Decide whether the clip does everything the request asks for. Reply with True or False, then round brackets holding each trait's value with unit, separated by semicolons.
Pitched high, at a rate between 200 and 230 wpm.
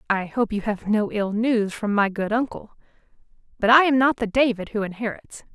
True (220 Hz; 205 wpm)